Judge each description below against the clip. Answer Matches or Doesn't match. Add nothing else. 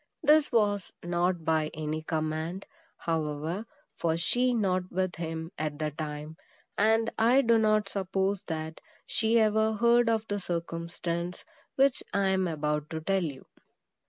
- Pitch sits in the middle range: Matches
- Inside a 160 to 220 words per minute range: Doesn't match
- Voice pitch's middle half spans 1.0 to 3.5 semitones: Doesn't match